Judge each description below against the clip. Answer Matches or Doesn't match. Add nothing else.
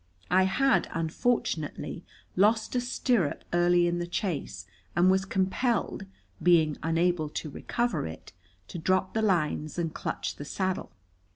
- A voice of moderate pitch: Matches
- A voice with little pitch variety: Doesn't match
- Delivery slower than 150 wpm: Matches